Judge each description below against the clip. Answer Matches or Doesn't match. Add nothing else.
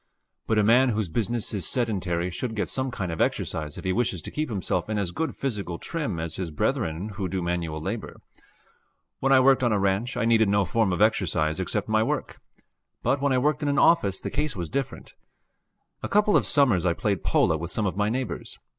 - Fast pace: Matches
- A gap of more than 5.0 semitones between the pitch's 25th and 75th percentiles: Matches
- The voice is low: Matches